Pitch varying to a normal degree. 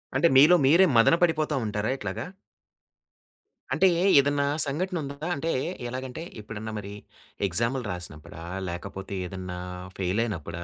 No: wide, 7.2 semitones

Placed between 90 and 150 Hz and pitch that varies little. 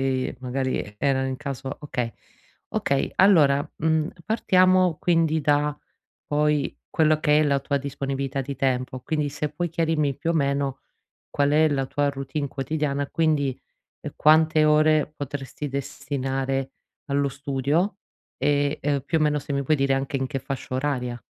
Yes: medium, 140 Hz; narrow, 2.1 semitones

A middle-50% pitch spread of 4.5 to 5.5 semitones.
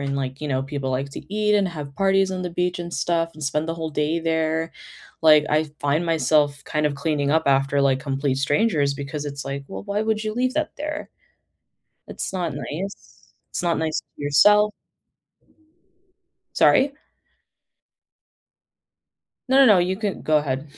Yes: average, 5.0 semitones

